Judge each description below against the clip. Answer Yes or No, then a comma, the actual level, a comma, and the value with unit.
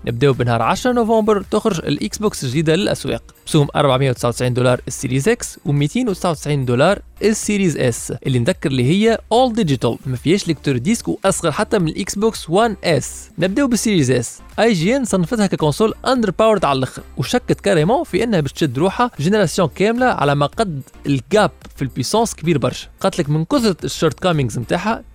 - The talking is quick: Yes, fast, 170 wpm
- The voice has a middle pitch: Yes, medium, 175 Hz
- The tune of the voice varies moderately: No, wide, 7.4 semitones